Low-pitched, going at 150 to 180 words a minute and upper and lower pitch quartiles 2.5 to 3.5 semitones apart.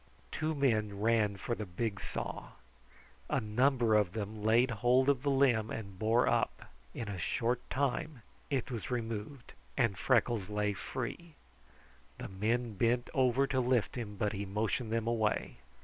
Yes: low, 115 Hz; average, 160 wpm; average, 3.2 semitones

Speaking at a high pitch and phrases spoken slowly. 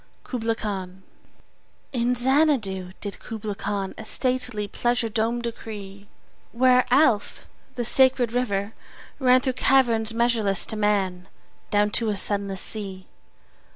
Yes: high, 220 Hz; slow, 120 wpm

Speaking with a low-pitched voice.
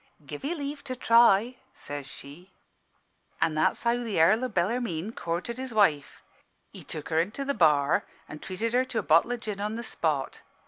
No: high, 210 Hz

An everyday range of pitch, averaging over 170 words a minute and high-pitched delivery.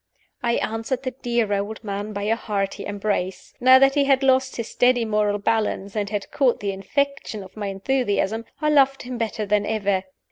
Yes: average, 4.1 semitones; average, 190 wpm; high, 220 Hz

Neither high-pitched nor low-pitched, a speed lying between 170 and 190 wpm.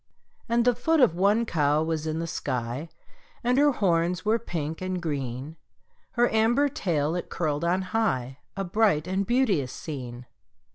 No: medium, 175 Hz; average, 160 wpm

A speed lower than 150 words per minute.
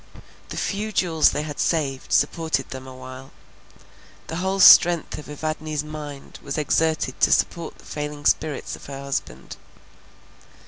Yes: average, 140 wpm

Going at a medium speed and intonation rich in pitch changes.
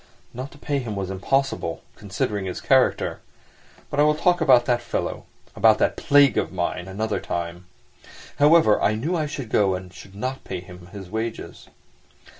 Yes: average, 175 wpm; wide, 6.5 semitones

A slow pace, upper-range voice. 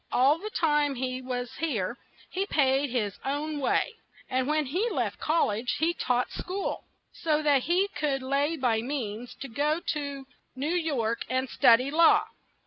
No: average, 170 wpm; very high, 280 Hz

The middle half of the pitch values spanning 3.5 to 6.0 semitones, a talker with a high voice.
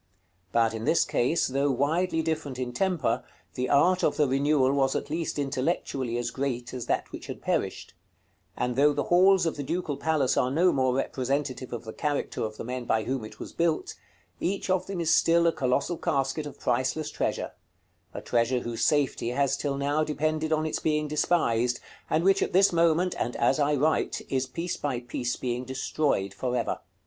No: average, 4.0 semitones; medium, 140 Hz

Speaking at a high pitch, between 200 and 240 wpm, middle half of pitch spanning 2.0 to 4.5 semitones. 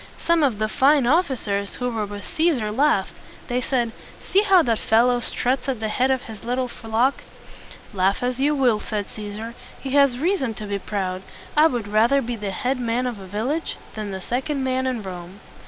Yes: high, 240 Hz; fast, 205 wpm; average, 4.1 semitones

